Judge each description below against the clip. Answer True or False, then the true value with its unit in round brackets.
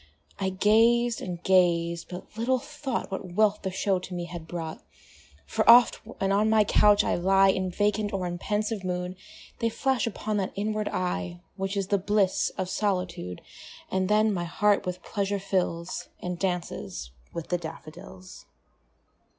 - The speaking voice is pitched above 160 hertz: True (190 Hz)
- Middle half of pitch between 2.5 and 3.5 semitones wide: True (2.8 semitones)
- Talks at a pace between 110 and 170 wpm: True (165 wpm)